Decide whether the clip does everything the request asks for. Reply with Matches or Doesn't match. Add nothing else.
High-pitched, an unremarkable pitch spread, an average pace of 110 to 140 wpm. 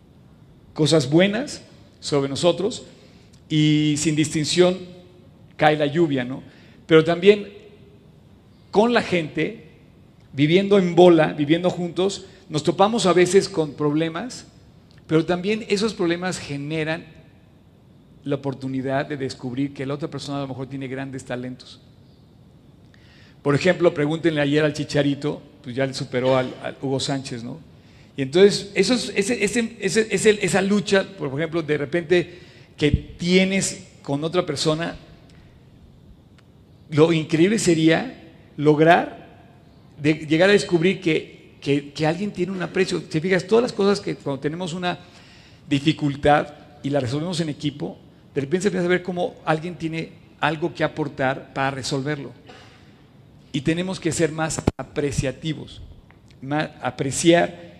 Doesn't match